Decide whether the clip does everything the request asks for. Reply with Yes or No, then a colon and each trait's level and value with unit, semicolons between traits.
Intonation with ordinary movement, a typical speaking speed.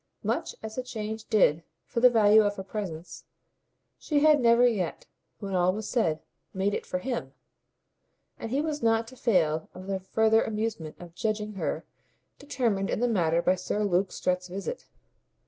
Yes: average, 3.9 semitones; average, 175 wpm